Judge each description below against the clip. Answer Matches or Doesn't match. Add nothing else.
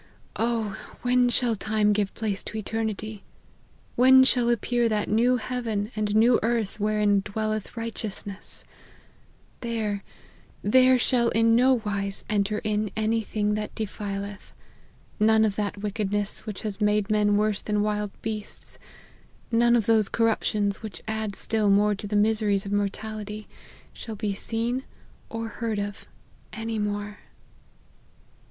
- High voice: Matches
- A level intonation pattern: Matches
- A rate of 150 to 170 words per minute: Doesn't match